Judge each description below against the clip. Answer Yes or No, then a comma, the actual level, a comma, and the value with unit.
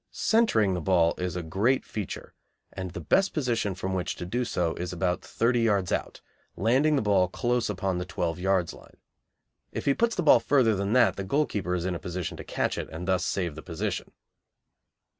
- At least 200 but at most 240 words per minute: Yes, fast, 205 wpm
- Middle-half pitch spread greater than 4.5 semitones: Yes, average, 4.9 semitones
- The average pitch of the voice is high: No, very low, 95 Hz